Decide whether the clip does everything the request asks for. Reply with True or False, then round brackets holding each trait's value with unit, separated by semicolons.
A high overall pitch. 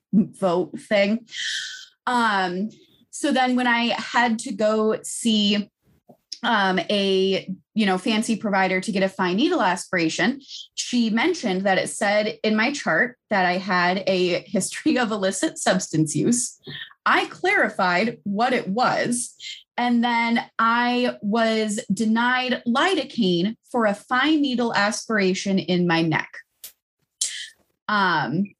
True (215 Hz)